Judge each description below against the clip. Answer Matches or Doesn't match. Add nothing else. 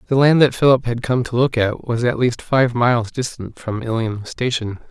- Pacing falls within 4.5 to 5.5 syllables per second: Matches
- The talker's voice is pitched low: Matches